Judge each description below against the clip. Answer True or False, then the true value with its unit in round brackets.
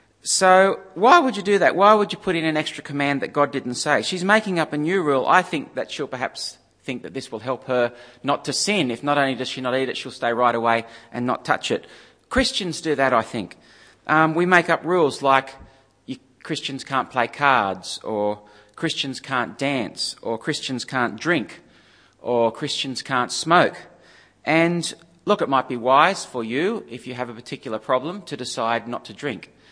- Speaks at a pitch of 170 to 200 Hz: False (135 Hz)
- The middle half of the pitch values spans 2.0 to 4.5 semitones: False (5.1 semitones)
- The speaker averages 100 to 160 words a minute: False (200 wpm)